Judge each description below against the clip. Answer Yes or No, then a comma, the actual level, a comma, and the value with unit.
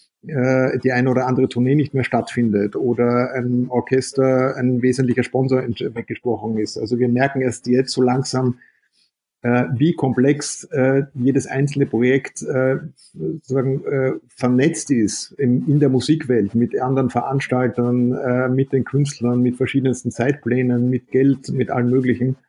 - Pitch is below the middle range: Yes, low, 130 Hz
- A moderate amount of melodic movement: No, narrow, 1.5 semitones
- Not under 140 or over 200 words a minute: No, average, 130 wpm